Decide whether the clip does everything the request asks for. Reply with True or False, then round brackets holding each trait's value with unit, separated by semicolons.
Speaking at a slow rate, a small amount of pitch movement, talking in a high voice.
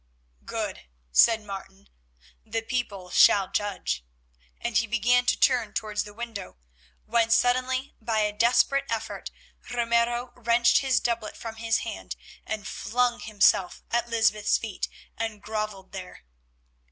True (130 wpm; 2.3 semitones; 225 Hz)